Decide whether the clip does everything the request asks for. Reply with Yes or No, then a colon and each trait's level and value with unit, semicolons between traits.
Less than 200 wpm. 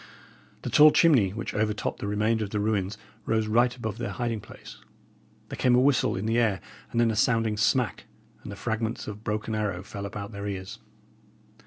No: fast, 205 wpm